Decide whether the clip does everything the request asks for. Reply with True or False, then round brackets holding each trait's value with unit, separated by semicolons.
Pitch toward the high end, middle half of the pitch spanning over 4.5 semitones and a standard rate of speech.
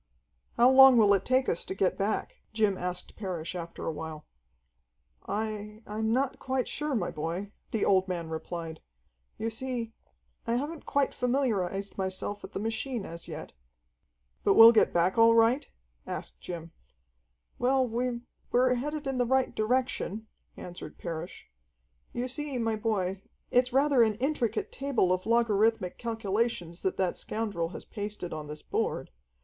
True (220 Hz; 5.1 semitones; 155 wpm)